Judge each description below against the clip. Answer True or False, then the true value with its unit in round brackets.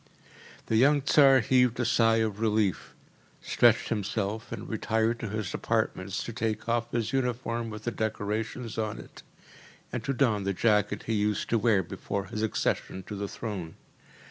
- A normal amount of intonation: False (2.1 semitones)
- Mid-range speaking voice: False (110 Hz)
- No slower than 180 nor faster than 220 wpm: False (170 wpm)